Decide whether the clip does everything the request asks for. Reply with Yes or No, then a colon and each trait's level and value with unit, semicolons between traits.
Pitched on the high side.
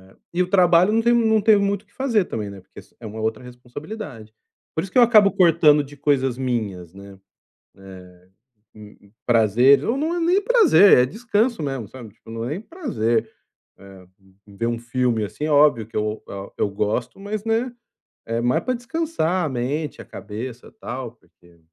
No: low, 135 Hz